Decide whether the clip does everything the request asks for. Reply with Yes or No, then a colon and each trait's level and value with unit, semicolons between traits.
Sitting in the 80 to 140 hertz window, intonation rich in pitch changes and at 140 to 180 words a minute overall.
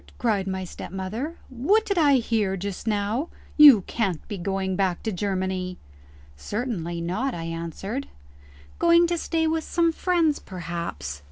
No: high, 205 Hz; wide, 7.6 semitones; average, 145 wpm